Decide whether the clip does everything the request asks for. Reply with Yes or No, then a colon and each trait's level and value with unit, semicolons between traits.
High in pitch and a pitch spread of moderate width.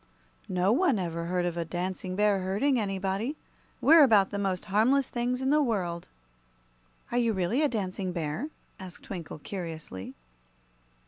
Yes: high, 195 Hz; average, 5.0 semitones